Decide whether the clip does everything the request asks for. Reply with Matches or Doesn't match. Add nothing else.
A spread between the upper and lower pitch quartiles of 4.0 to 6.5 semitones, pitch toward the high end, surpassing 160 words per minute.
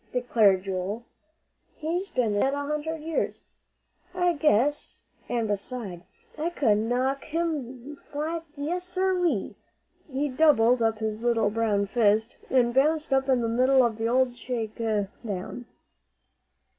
Doesn't match